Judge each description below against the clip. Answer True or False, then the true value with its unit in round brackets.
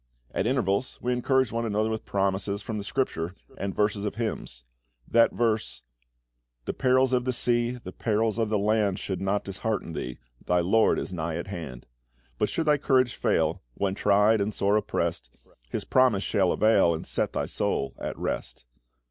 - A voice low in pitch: True (105 Hz)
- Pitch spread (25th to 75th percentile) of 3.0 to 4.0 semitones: True (3.5 semitones)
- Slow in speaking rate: False (180 wpm)